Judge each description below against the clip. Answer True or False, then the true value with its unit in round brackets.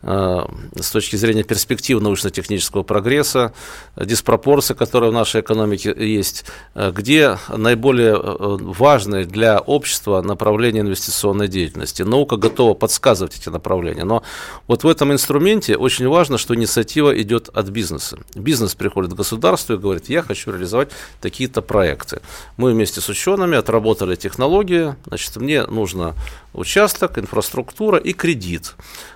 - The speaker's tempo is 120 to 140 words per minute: True (125 wpm)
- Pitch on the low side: True (110 Hz)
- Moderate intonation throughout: True (4.3 semitones)